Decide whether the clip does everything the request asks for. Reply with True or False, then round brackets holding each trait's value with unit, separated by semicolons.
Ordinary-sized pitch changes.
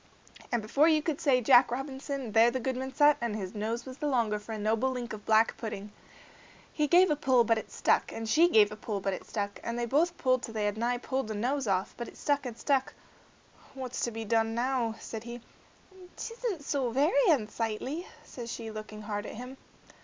True (3.8 semitones)